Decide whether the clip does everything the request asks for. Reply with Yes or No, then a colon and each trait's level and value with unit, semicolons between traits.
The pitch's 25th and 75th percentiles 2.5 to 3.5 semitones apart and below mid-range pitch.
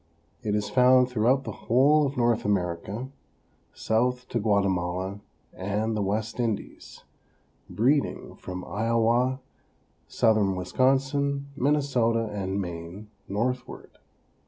No: average, 4.2 semitones; low, 115 Hz